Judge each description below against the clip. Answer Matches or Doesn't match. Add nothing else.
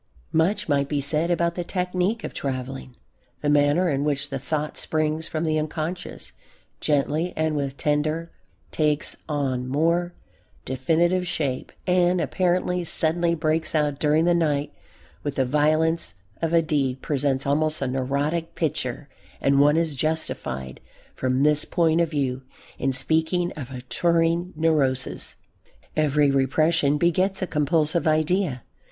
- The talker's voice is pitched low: Doesn't match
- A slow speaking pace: Doesn't match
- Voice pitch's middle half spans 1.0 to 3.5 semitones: Matches